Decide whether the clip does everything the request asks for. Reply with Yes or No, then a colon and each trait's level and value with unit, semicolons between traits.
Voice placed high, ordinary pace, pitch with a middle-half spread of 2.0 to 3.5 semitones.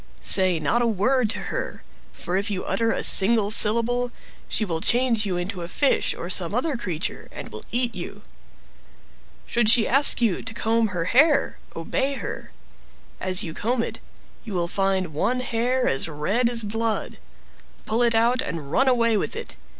No: high, 225 Hz; average, 175 wpm; average, 4.4 semitones